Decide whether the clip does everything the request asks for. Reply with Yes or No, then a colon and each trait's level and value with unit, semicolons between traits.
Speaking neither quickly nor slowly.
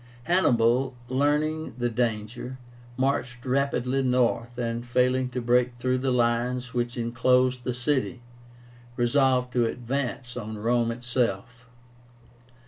No: slow, 115 wpm